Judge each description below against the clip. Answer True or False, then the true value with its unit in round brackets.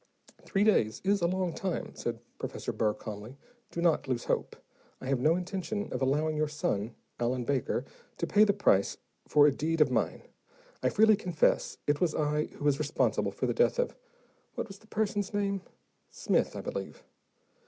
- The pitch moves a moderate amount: False (6.6 semitones)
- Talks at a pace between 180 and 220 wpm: True (185 wpm)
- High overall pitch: False (155 Hz)